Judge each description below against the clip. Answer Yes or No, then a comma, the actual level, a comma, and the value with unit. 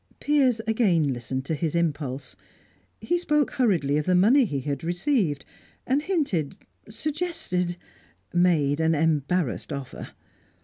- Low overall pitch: No, medium, 175 Hz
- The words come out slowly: Yes, slow, 125 wpm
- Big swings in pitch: Yes, wide, 9.0 semitones